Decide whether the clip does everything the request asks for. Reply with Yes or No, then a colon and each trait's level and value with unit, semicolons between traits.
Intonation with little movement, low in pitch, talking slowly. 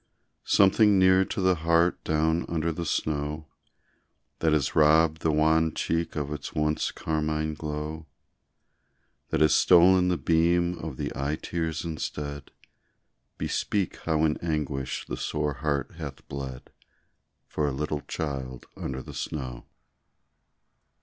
Yes: narrow, 2.0 semitones; very low, 80 Hz; slow, 130 wpm